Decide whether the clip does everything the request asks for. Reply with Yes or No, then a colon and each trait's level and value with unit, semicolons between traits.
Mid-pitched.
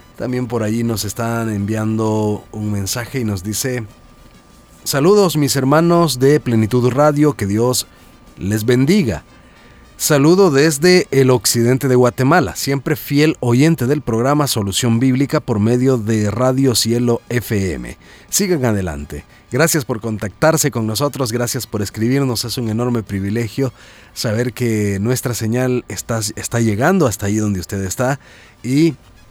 No: low, 120 Hz